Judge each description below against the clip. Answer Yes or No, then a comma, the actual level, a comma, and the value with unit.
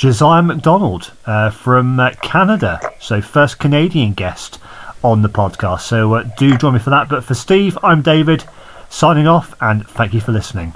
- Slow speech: No, average, 180 wpm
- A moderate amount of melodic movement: No, wide, 6.2 semitones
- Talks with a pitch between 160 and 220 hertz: No, low, 125 Hz